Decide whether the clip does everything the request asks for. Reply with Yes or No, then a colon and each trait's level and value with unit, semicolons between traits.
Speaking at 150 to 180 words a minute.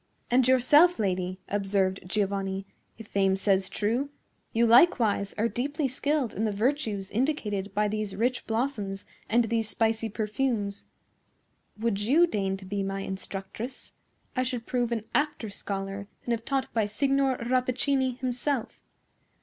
No: average, 140 wpm